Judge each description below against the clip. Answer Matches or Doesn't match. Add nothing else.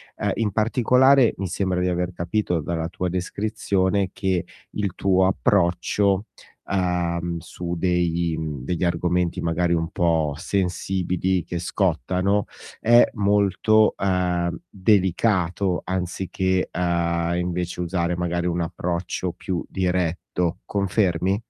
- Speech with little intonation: Matches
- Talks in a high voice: Doesn't match